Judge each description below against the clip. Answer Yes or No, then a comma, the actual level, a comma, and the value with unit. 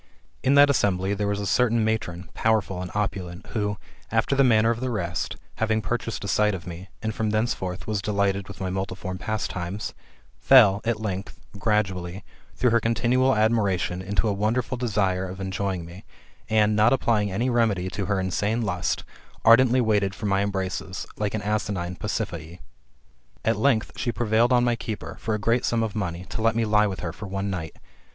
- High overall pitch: No, low, 105 Hz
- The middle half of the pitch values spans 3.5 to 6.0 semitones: No, average, 3.0 semitones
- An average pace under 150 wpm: No, average, 190 wpm